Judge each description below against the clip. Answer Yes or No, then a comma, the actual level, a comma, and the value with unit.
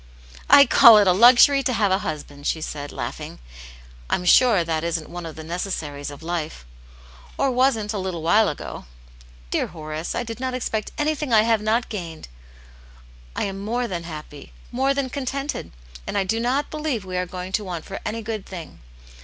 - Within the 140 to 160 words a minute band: No, average, 195 wpm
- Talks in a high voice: Yes, high, 195 Hz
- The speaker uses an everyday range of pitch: No, wide, 6.7 semitones